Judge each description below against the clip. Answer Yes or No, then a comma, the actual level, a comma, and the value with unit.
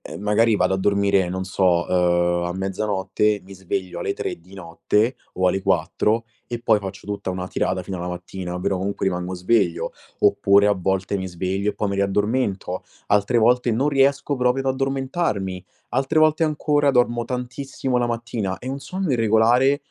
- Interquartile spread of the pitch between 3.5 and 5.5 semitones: Yes, average, 4.8 semitones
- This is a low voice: Yes, low, 100 Hz